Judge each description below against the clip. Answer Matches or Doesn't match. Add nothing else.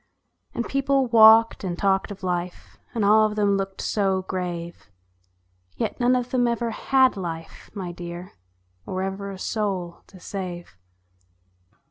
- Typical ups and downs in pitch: Matches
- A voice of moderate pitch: Doesn't match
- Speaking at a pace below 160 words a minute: Matches